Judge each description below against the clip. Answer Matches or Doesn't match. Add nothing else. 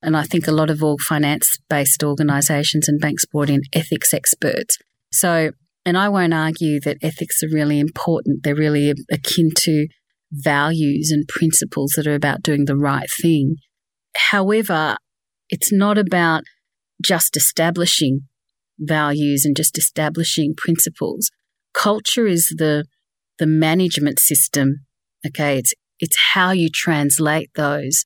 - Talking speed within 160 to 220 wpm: Doesn't match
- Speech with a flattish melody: Matches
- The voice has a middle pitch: Matches